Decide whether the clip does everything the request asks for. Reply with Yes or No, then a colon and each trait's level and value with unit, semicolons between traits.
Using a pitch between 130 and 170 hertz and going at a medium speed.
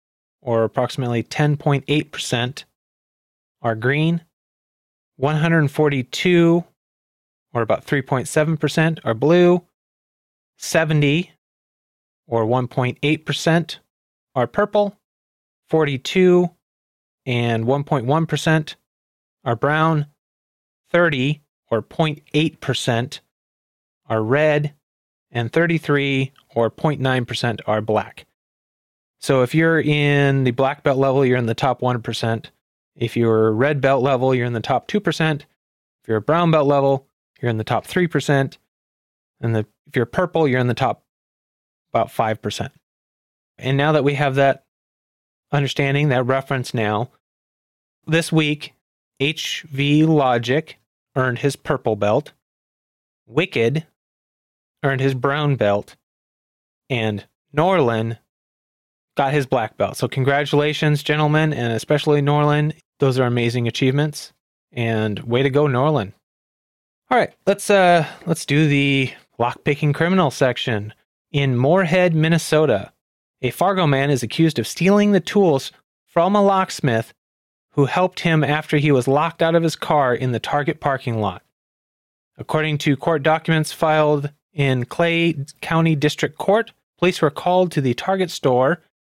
No: medium, 140 Hz; slow, 125 wpm